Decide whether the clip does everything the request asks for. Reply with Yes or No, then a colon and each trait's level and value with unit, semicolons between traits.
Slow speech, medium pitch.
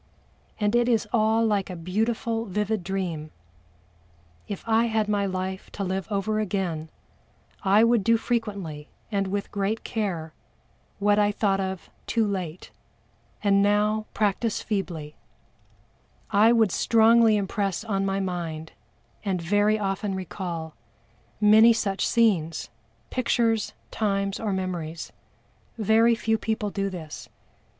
No: slow, 125 wpm; high, 200 Hz